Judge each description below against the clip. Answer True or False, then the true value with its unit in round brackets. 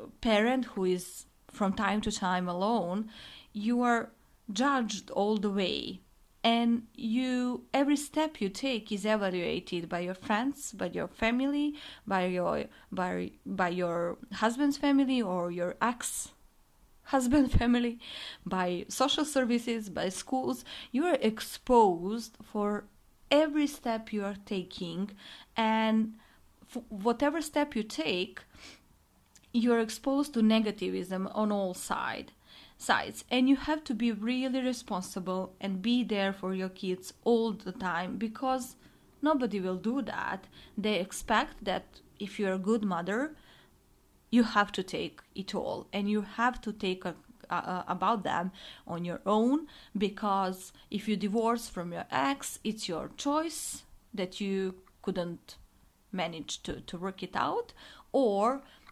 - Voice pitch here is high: True (215 Hz)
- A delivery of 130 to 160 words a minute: True (140 wpm)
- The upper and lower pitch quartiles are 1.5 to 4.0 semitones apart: False (4.6 semitones)